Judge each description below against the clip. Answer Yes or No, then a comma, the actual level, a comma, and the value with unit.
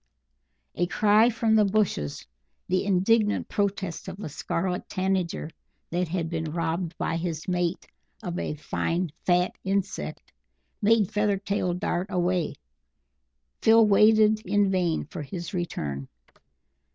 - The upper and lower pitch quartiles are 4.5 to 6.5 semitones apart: No, average, 3.2 semitones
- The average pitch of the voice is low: No, medium, 185 Hz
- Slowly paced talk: Yes, slow, 125 wpm